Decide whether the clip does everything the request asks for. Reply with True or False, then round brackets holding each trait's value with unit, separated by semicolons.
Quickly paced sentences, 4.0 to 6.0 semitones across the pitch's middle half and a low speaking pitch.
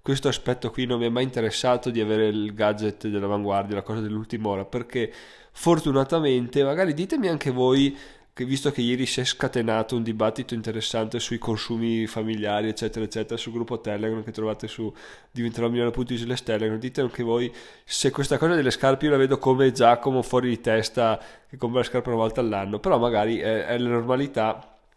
False (185 wpm; 2.6 semitones; 120 Hz)